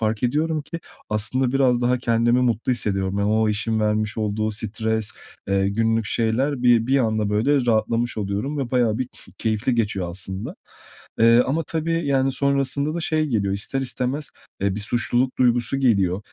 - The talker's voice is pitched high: No, low, 115 Hz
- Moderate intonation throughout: Yes, average, 3.7 semitones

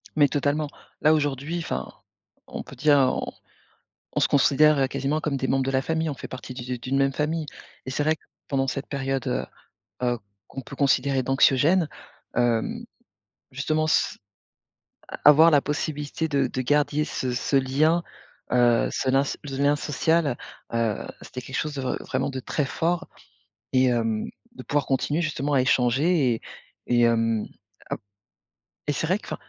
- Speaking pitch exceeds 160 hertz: No, medium, 140 Hz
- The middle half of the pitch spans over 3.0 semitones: No, average, 2.7 semitones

